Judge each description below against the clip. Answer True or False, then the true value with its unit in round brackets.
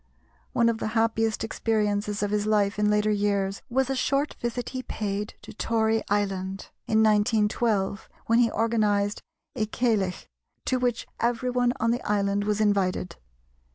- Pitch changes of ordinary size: False (2.2 semitones)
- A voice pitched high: True (215 Hz)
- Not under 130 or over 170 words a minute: True (155 wpm)